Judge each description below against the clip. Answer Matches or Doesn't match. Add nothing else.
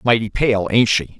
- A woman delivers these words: Doesn't match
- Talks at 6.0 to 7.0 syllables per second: Doesn't match